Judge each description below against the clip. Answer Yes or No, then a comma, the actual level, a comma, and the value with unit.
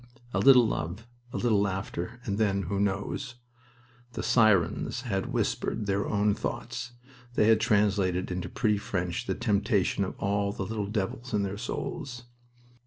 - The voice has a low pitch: Yes, low, 100 Hz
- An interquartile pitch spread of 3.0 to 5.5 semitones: No, narrow, 2.4 semitones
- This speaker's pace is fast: No, average, 155 wpm